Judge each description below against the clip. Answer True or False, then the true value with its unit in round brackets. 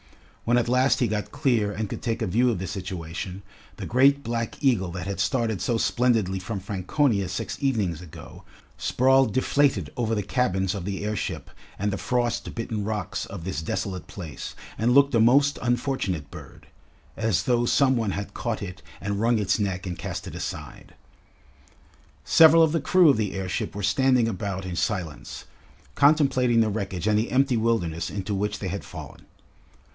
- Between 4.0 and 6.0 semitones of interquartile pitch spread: True (4.4 semitones)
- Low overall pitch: True (110 Hz)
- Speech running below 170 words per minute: False (180 wpm)